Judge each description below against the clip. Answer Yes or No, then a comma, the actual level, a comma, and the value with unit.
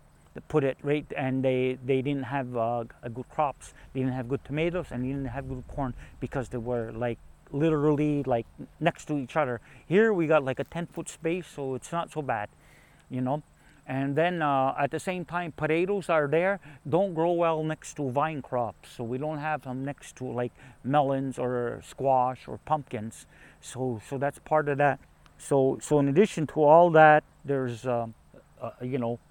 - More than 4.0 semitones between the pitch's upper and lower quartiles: No, average, 3.3 semitones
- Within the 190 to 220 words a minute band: Yes, average, 200 wpm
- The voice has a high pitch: No, medium, 140 Hz